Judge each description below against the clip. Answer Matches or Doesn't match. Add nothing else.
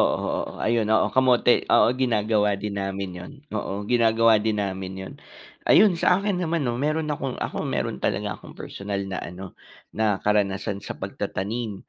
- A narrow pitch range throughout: Doesn't match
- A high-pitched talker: Doesn't match